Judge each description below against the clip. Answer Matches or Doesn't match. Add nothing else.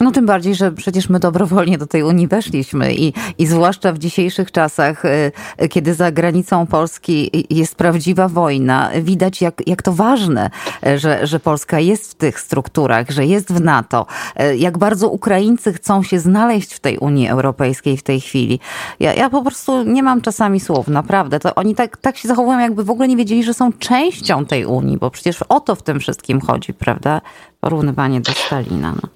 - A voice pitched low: Doesn't match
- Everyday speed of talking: Doesn't match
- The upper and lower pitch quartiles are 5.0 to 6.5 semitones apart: Matches